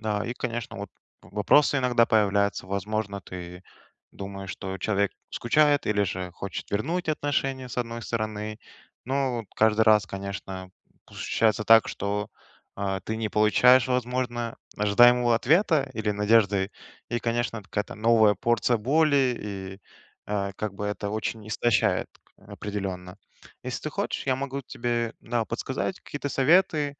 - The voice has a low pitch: Yes, low, 110 Hz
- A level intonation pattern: No, average, 3.4 semitones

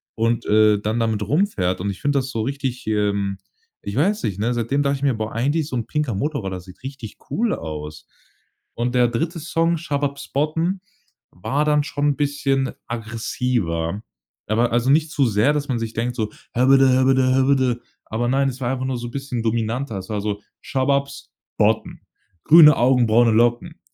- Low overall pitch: Yes, low, 125 Hz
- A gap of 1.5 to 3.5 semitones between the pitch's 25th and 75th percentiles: No, average, 4.2 semitones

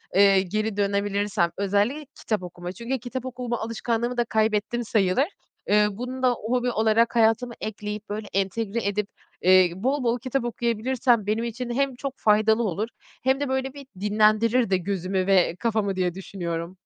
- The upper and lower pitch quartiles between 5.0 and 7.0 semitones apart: No, average, 3.3 semitones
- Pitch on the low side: No, high, 220 Hz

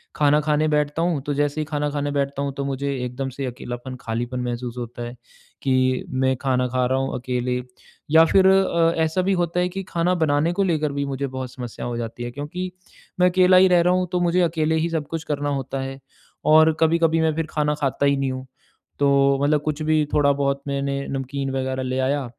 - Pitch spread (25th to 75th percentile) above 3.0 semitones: Yes, average, 3.5 semitones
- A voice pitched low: No, medium, 145 Hz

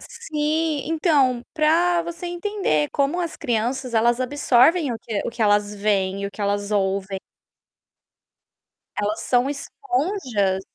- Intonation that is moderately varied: No, wide, 7.6 semitones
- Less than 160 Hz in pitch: No, very high, 250 Hz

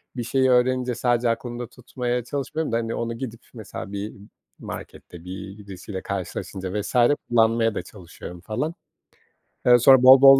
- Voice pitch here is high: No, low, 115 Hz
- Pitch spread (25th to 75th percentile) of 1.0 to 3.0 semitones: No, average, 3.6 semitones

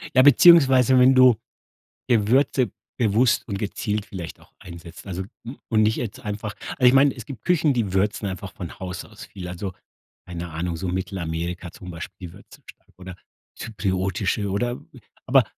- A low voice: Yes, low, 100 Hz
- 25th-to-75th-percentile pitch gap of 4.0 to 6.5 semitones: Yes, average, 5.1 semitones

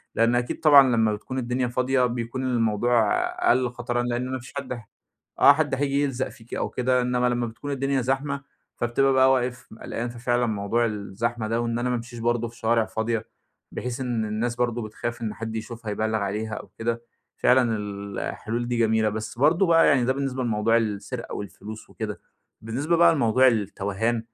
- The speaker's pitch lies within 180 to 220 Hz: No, low, 120 Hz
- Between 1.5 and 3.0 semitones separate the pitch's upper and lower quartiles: Yes, narrow, 2.4 semitones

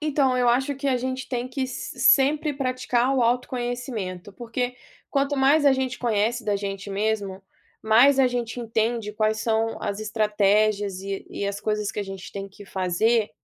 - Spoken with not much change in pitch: No, average, 3.8 semitones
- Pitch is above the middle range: Yes, high, 230 Hz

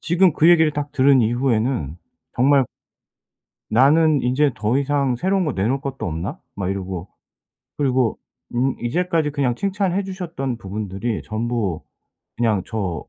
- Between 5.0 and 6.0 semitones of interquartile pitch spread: Yes, wide, 5.6 semitones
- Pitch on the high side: No, low, 130 Hz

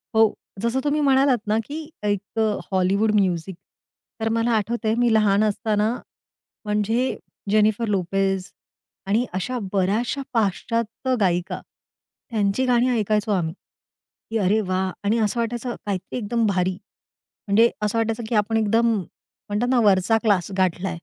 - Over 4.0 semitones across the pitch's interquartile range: No, average, 3.0 semitones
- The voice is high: Yes, high, 215 Hz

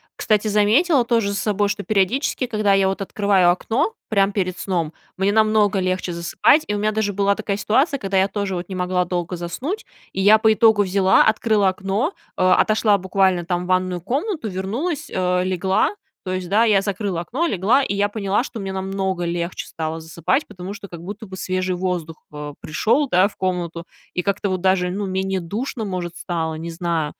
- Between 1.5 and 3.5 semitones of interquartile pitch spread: Yes, average, 2.9 semitones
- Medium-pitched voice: No, high, 195 Hz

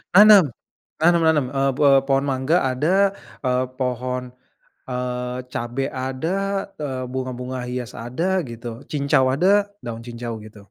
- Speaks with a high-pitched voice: No, low, 130 Hz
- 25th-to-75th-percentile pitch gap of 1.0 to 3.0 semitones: Yes, average, 2.7 semitones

